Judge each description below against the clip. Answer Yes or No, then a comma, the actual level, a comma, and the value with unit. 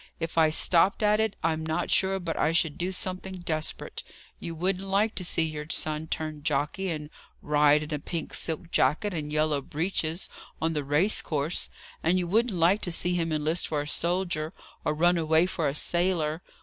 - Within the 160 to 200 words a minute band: Yes, average, 195 wpm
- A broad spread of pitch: No, average, 2.9 semitones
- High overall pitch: No, medium, 165 Hz